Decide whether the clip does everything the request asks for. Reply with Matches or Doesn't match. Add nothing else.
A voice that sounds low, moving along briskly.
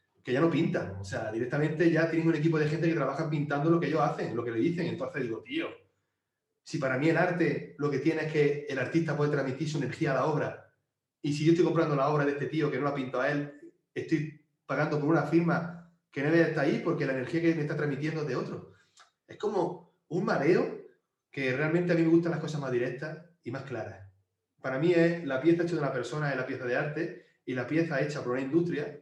Doesn't match